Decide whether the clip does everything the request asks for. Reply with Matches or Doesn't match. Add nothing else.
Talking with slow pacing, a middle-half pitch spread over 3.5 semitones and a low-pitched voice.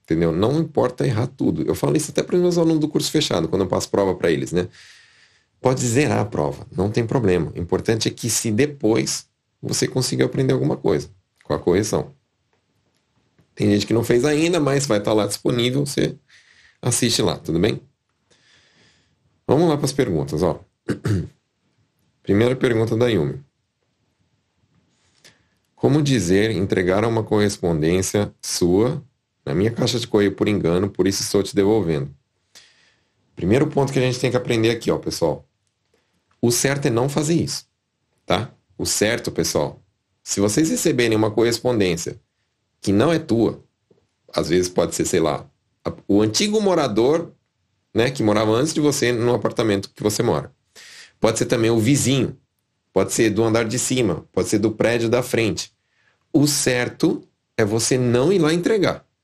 Doesn't match